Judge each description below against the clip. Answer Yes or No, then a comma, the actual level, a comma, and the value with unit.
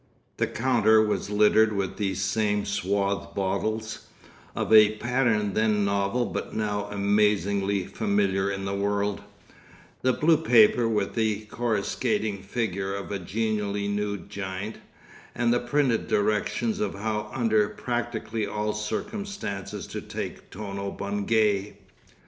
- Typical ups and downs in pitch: No, narrow, 1.9 semitones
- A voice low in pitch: Yes, low, 105 Hz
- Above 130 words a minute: No, slow, 125 wpm